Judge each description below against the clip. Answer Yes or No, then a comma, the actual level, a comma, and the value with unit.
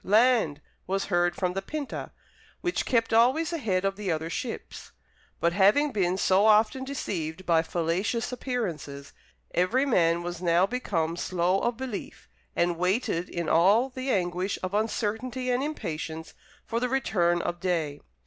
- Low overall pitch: No, high, 195 Hz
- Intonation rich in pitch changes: Yes, wide, 5.9 semitones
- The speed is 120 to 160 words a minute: Yes, average, 150 wpm